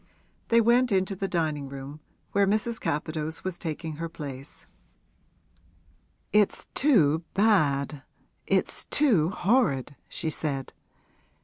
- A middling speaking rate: No, slow, 110 wpm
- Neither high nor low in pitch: Yes, medium, 165 Hz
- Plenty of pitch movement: Yes, wide, 5.9 semitones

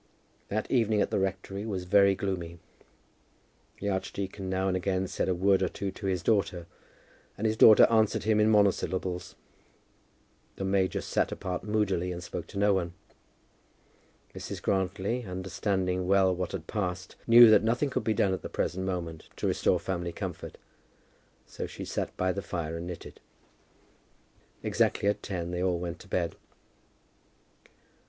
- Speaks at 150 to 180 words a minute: Yes, average, 160 wpm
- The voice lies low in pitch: Yes, very low, 95 Hz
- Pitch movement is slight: Yes, narrow, 2.0 semitones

